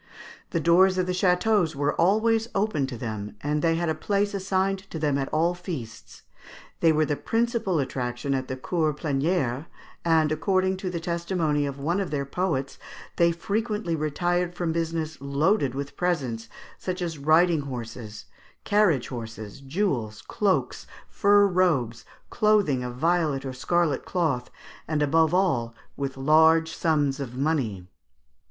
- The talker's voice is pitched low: No, medium, 160 Hz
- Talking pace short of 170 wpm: Yes, average, 150 wpm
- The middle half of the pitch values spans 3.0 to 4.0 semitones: No, average, 4.8 semitones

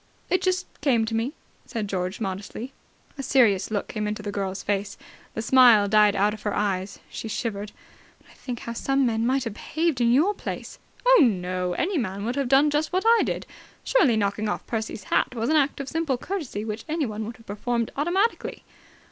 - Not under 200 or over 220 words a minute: Yes, fast, 205 wpm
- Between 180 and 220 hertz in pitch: No, high, 230 Hz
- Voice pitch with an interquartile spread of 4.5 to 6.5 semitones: Yes, average, 5.0 semitones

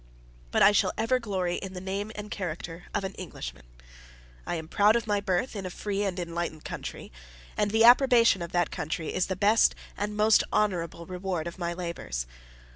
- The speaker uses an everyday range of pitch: Yes, average, 3.4 semitones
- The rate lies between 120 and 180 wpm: No, average, 195 wpm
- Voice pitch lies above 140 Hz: Yes, high, 190 Hz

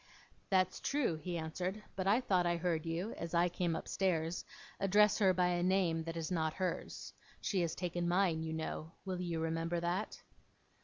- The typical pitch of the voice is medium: Yes, medium, 175 Hz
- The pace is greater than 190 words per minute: No, average, 185 wpm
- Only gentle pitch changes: Yes, narrow, 2.3 semitones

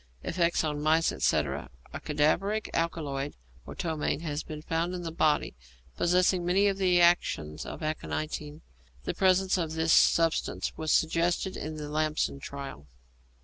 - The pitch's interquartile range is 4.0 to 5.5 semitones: No, average, 2.8 semitones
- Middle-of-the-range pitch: Yes, medium, 160 Hz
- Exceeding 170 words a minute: No, average, 145 wpm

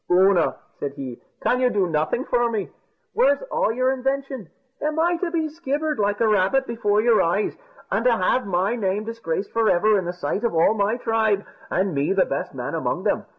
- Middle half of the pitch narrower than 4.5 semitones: No, average, 5.2 semitones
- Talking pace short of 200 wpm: No, fast, 205 wpm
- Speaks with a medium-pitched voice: No, high, 215 Hz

